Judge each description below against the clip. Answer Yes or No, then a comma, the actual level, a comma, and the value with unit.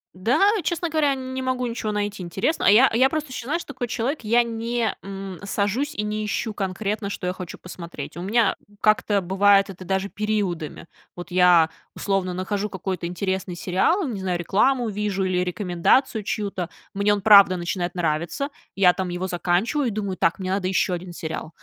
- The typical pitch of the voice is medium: No, high, 200 Hz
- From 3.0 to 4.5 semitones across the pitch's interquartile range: Yes, average, 3.9 semitones